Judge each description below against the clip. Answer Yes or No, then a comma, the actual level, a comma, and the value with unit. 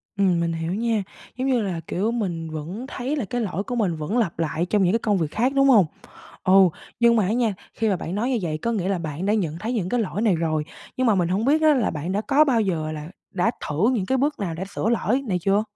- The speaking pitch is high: Yes, high, 200 Hz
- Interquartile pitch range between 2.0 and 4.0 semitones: No, wide, 5.5 semitones